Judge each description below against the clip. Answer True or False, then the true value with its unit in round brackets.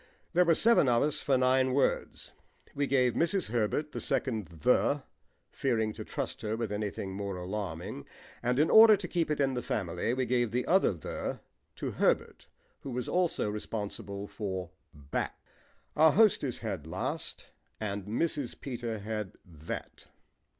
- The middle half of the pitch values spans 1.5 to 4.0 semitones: False (5.6 semitones)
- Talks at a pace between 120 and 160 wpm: True (155 wpm)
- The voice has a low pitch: True (115 Hz)